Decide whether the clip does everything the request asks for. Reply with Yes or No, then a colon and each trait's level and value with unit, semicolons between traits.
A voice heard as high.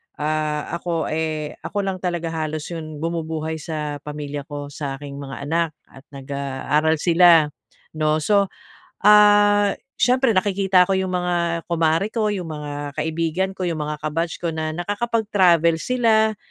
No: medium, 165 Hz